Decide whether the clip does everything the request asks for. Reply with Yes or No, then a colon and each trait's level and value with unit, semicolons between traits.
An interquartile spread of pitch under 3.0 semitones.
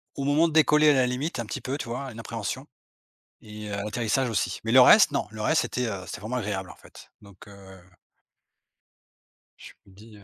No: average, 4.4 semitones